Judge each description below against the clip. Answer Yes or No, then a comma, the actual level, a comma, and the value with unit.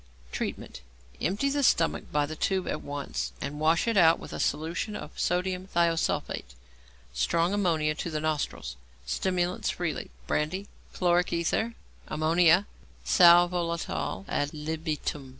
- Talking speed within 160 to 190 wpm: No, slow, 135 wpm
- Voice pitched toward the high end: No, medium, 165 Hz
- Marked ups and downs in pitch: No, average, 2.9 semitones